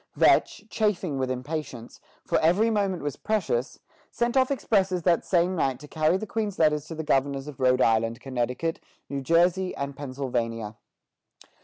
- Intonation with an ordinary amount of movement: No, wide, 6.1 semitones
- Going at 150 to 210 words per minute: Yes, average, 160 wpm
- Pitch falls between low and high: Yes, medium, 155 Hz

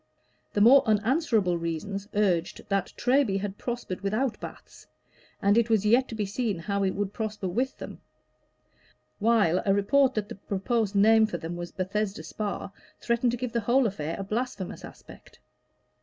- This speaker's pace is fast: No, average, 170 wpm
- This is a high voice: Yes, high, 210 Hz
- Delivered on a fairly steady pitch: No, average, 3.3 semitones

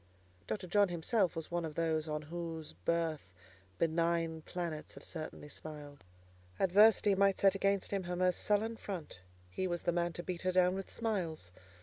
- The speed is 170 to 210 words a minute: Yes, average, 175 wpm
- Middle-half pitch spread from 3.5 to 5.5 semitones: No, average, 3.1 semitones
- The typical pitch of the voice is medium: Yes, medium, 175 Hz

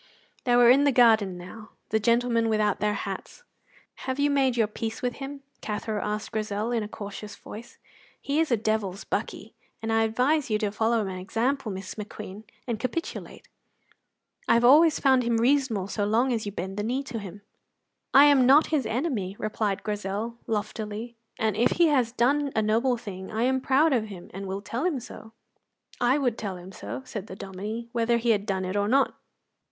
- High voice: Yes, high, 225 Hz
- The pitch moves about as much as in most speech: Yes, average, 3.5 semitones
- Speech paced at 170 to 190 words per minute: No, average, 200 wpm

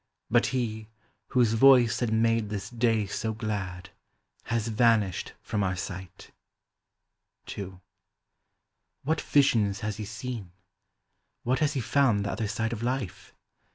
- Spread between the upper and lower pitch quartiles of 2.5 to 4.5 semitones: Yes, average, 2.9 semitones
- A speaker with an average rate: No, slow, 130 wpm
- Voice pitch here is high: No, low, 110 Hz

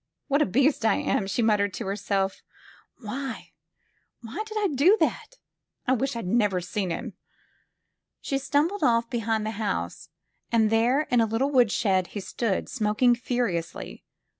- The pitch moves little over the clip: No, average, 4.5 semitones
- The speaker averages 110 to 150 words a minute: No, average, 165 wpm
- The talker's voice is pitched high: Yes, high, 230 Hz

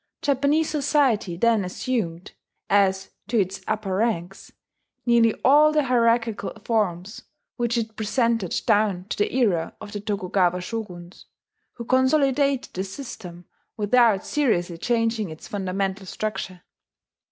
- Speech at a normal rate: No, slow, 120 wpm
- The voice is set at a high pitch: Yes, high, 215 Hz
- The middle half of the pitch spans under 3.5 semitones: No, average, 4.1 semitones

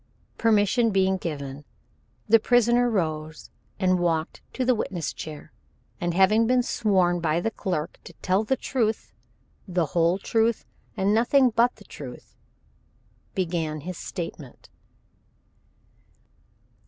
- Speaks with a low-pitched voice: No, high, 190 Hz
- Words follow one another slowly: Yes, slow, 120 wpm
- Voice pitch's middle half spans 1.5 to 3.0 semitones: No, average, 5.3 semitones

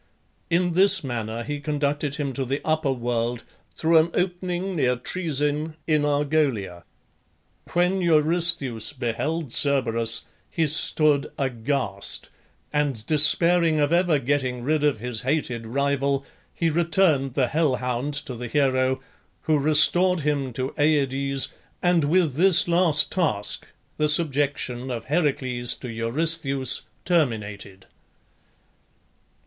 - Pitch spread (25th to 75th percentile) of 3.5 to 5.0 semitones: Yes, average, 4.1 semitones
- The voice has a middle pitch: Yes, medium, 145 Hz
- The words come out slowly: Yes, slow, 120 wpm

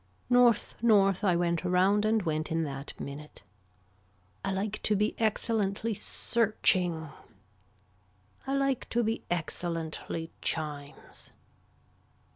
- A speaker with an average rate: No, slow, 105 wpm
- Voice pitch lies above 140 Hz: Yes, high, 190 Hz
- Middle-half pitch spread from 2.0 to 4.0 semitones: No, average, 5.0 semitones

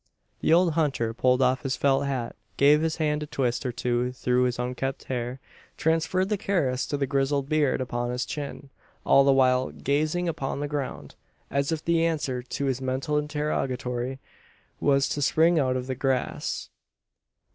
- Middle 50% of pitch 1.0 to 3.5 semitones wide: Yes, average, 2.9 semitones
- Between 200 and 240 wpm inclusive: No, average, 175 wpm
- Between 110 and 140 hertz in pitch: Yes, low, 135 Hz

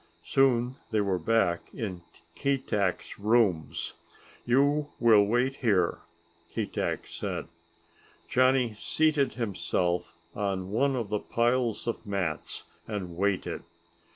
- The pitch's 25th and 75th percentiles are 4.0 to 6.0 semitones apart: Yes, average, 4.6 semitones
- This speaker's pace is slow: Yes, slow, 105 wpm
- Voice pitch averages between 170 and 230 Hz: No, low, 110 Hz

